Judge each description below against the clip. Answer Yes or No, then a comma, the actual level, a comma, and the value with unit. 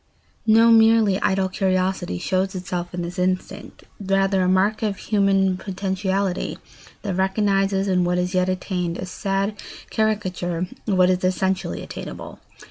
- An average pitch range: No, narrow, 1.3 semitones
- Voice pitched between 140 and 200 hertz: Yes, high, 190 Hz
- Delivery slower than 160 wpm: Yes, average, 140 wpm